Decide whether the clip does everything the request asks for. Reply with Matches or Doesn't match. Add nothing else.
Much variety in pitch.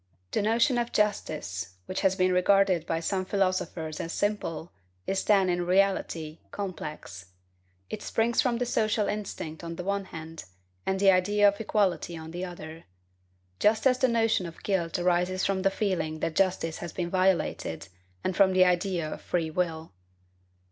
Doesn't match